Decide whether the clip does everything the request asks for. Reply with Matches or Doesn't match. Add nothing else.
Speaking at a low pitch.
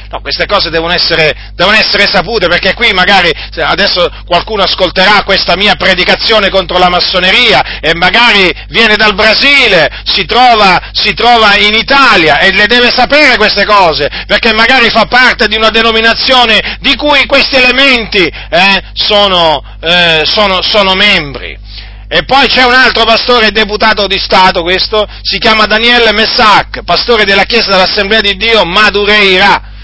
Doesn't match